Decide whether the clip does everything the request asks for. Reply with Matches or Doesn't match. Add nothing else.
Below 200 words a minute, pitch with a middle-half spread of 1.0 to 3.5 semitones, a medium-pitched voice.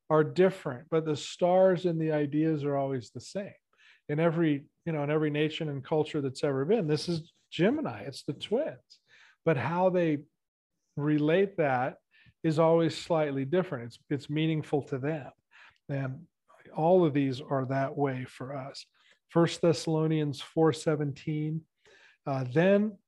Matches